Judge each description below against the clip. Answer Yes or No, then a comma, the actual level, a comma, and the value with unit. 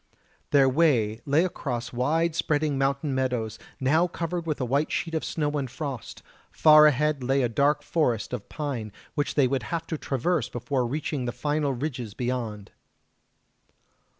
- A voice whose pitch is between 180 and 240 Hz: No, medium, 140 Hz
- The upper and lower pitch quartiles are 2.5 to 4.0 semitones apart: Yes, average, 3.7 semitones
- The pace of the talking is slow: No, average, 160 wpm